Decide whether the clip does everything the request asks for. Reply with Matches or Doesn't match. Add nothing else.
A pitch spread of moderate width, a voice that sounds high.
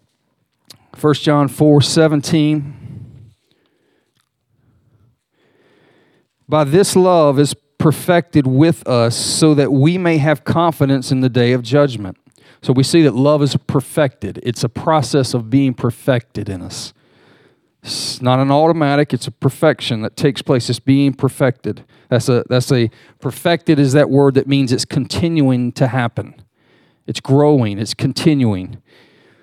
Doesn't match